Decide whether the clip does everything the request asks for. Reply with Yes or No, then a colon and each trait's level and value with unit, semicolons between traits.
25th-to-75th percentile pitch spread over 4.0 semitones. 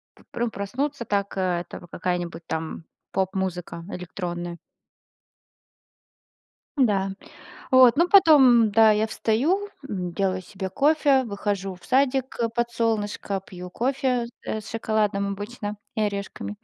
Yes: average, 4.5 semitones